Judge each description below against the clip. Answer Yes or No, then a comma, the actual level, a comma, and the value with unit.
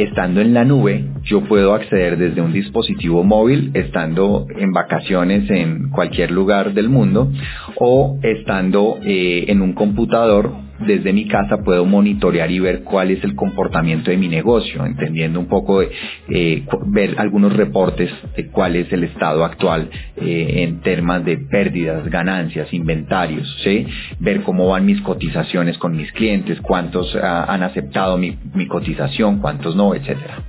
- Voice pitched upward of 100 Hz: No, very low, 90 Hz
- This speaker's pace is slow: No, average, 155 wpm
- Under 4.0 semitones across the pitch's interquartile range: Yes, average, 3.5 semitones